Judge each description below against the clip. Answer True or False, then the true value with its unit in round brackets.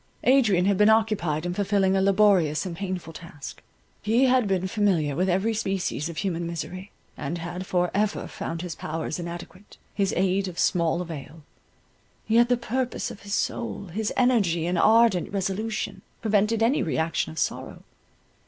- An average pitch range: True (3.9 semitones)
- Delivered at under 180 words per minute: True (165 wpm)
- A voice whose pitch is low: False (190 Hz)